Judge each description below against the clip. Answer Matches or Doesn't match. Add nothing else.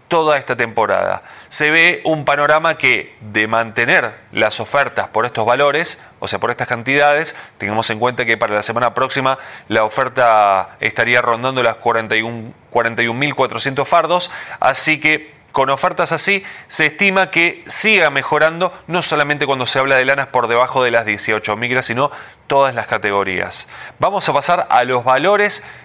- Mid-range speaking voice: Doesn't match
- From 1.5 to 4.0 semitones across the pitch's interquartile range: Doesn't match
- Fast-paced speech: Doesn't match